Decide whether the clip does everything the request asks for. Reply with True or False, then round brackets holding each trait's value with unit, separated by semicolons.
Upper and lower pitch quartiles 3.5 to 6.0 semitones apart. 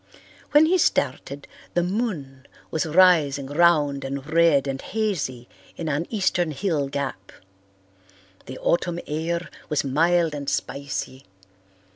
True (3.9 semitones)